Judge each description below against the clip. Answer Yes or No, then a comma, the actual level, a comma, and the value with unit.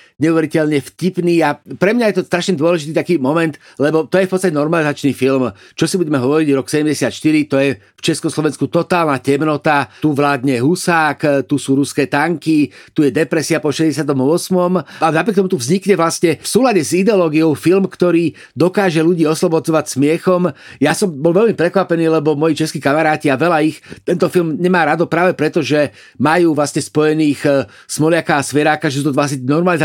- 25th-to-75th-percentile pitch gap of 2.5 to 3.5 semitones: Yes, average, 2.9 semitones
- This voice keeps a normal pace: No, fast, 175 wpm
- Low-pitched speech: No, medium, 155 Hz